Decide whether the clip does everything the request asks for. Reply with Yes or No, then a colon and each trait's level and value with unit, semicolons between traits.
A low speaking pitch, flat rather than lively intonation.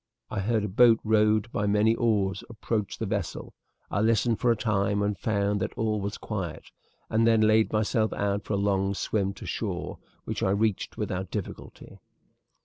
Yes: low, 105 Hz; narrow, 1.8 semitones